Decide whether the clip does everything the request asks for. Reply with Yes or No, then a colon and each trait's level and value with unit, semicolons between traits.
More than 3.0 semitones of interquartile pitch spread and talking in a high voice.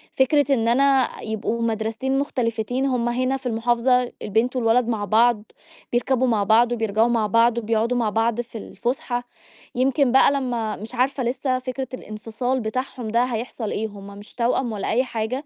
No: narrow, 2.4 semitones; high, 240 Hz